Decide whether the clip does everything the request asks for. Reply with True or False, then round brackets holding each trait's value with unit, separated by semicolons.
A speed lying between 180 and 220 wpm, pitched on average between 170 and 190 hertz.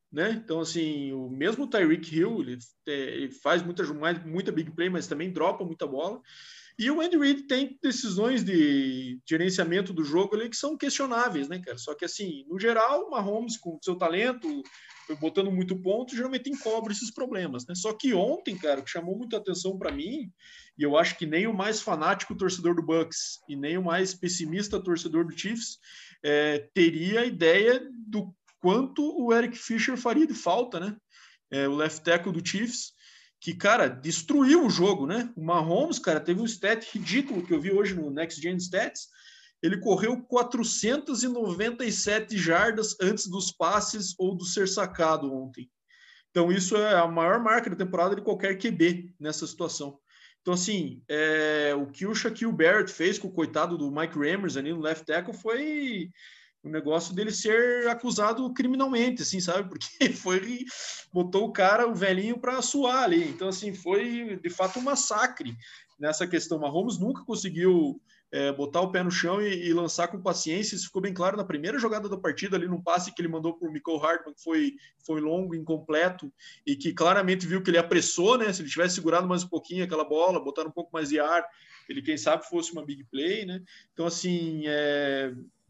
True (185 wpm; 185 Hz)